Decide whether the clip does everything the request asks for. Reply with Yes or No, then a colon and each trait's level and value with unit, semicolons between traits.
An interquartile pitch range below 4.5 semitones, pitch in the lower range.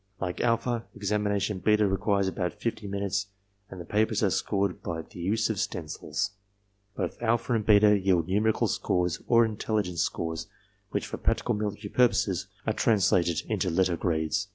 Yes: average, 2.9 semitones; low, 100 Hz